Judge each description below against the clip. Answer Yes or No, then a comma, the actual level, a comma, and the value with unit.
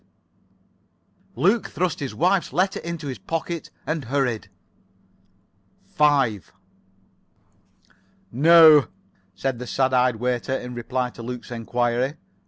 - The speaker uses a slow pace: Yes, slow, 105 wpm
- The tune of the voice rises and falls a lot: No, average, 4.5 semitones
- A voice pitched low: Yes, low, 130 Hz